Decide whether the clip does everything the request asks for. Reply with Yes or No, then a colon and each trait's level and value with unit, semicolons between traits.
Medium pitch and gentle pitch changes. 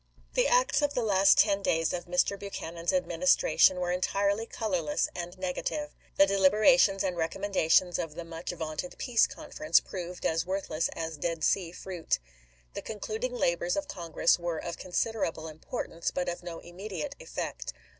No: medium, 180 Hz; average, 3.5 semitones